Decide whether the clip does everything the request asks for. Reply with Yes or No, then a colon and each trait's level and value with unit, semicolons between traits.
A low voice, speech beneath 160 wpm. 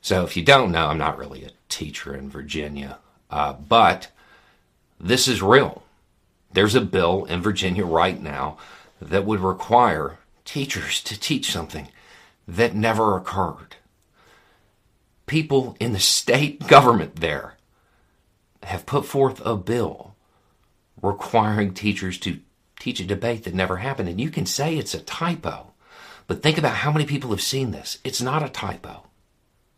Yes: low, 105 Hz; average, 150 wpm